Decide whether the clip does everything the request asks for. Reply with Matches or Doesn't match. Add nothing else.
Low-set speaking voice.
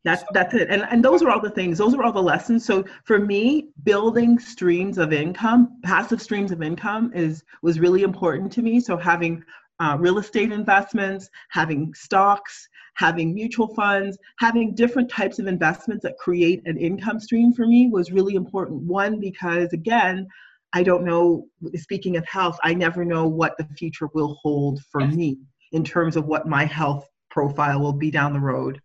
Doesn't match